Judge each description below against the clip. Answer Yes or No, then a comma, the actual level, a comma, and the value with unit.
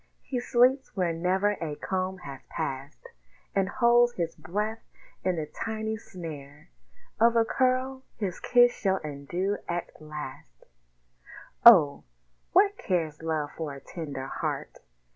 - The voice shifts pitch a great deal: Yes, wide, 7.0 semitones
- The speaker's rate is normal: No, slow, 130 wpm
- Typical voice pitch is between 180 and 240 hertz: Yes, medium, 185 Hz